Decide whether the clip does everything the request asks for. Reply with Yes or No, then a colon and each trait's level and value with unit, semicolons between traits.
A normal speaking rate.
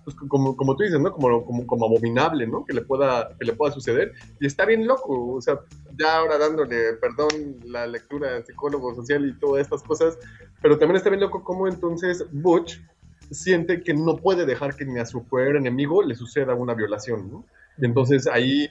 No: fast, 200 wpm